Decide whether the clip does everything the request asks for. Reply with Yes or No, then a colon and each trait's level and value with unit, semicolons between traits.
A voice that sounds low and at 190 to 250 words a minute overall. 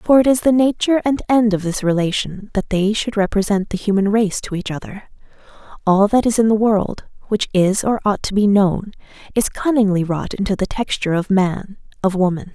No: high, 205 Hz; fast, 205 wpm